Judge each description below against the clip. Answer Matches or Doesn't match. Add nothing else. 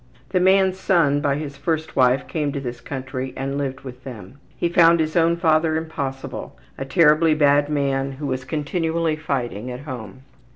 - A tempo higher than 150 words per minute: Matches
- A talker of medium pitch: Matches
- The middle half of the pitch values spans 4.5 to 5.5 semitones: Doesn't match